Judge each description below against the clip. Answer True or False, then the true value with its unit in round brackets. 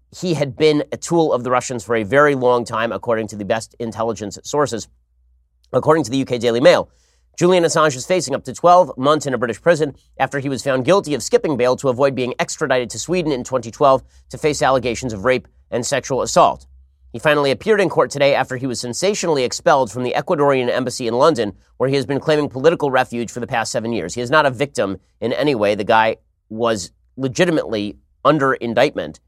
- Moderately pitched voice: False (130 Hz)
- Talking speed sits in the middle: False (215 wpm)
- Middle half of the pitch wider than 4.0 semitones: True (4.6 semitones)